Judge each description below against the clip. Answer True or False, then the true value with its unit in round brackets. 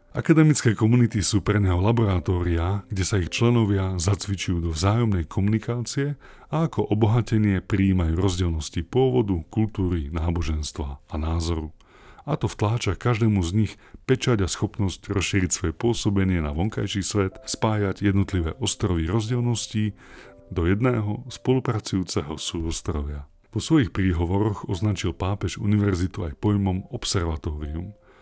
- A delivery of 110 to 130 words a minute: True (120 wpm)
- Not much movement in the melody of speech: False (3.9 semitones)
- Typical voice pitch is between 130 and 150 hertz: False (100 Hz)